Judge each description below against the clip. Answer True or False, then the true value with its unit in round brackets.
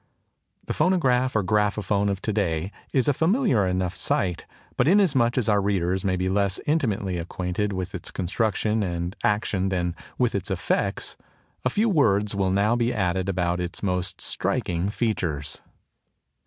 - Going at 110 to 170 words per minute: True (155 wpm)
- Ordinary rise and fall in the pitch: True (3.8 semitones)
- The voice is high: False (100 Hz)